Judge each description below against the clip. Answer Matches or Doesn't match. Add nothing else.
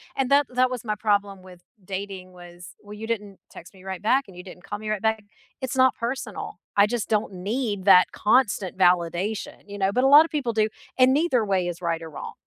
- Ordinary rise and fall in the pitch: Matches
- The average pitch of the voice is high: Matches